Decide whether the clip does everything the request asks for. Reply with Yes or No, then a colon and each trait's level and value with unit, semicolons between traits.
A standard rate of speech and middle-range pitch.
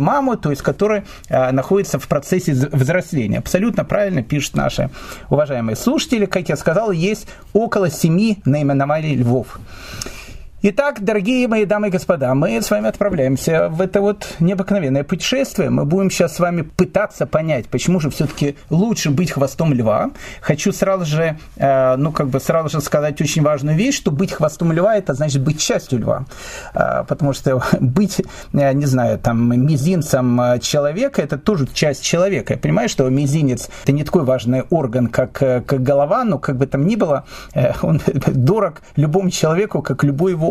No: fast, 165 wpm; medium, 155 Hz